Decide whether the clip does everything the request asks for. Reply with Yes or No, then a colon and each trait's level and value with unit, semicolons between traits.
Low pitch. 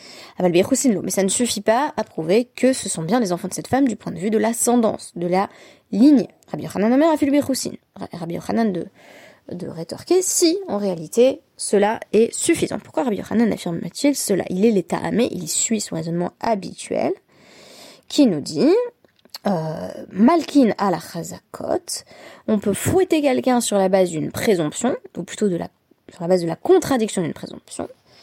No: high, 220 Hz